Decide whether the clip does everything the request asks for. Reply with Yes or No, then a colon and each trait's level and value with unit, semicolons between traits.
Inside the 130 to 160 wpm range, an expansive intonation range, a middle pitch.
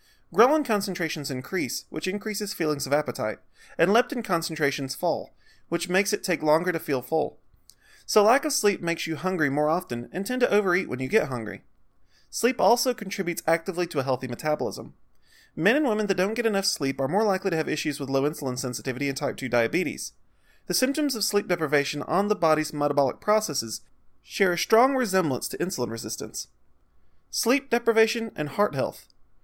No: average, 180 wpm; wide, 6.9 semitones; medium, 170 Hz